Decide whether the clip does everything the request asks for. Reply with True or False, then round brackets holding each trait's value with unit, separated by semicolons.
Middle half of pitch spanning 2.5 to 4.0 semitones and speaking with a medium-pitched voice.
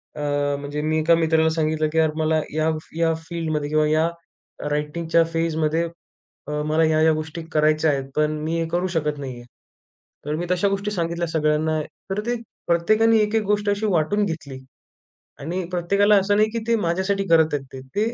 True (2.8 semitones; 160 Hz)